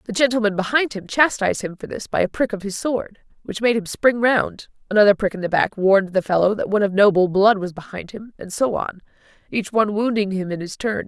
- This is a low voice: No, high, 205 Hz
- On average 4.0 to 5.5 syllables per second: No, 5.9 syllables/s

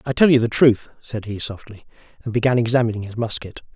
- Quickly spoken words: Yes, fast, 210 wpm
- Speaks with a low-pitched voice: Yes, low, 115 Hz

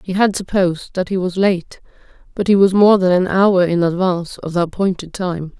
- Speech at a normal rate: No, fast, 215 wpm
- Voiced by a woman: Yes, female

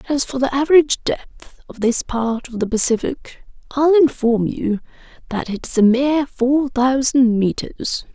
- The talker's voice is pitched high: Yes, very high, 255 Hz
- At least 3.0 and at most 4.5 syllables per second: Yes, 4.3 syllables/s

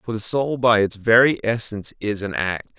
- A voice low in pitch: Yes, low, 110 Hz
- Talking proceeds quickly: Yes, fast, 215 wpm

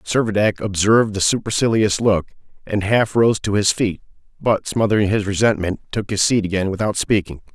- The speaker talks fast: No, average, 165 wpm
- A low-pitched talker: Yes, low, 105 Hz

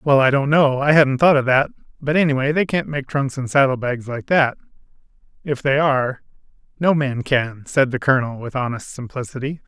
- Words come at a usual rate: Yes, average, 180 wpm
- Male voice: Yes, male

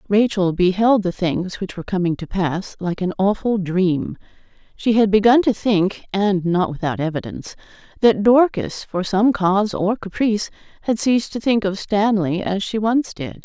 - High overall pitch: Yes, high, 200 Hz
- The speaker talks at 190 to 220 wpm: No, average, 175 wpm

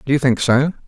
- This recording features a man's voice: Yes, male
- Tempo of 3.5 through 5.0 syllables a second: No, 6.3 syllables/s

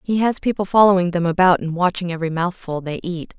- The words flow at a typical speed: No, fast, 215 wpm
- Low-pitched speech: No, medium, 180 Hz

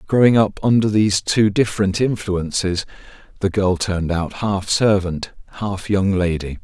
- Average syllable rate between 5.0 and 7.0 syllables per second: No, 4.6 syllables/s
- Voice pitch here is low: Yes, low, 100 Hz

